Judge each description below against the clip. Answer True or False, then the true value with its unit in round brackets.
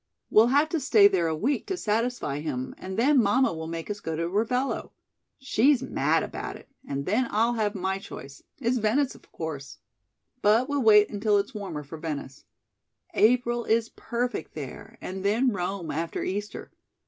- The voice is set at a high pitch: True (210 Hz)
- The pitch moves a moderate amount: False (6.3 semitones)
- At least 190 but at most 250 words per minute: False (175 wpm)